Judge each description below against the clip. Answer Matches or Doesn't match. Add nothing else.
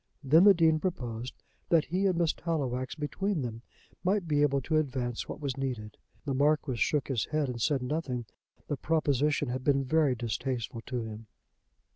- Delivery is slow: Doesn't match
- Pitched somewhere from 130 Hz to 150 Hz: Matches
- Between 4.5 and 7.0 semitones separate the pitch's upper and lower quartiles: Doesn't match